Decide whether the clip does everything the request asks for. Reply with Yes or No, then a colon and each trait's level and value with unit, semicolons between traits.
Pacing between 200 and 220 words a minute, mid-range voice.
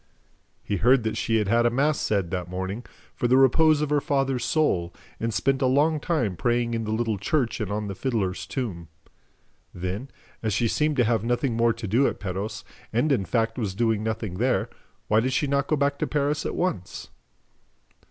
No: fast, 205 wpm; low, 115 Hz